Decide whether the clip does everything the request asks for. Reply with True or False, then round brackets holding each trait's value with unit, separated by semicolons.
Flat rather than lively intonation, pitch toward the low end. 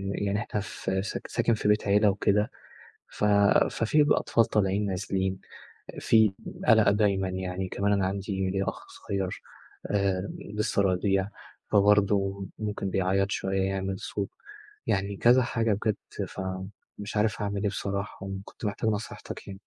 True (1.4 semitones; 100 Hz)